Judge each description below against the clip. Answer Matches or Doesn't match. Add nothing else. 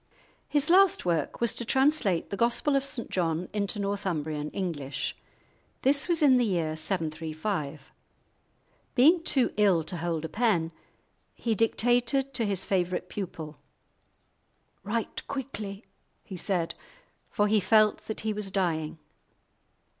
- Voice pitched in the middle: Doesn't match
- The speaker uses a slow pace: Matches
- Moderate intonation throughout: Doesn't match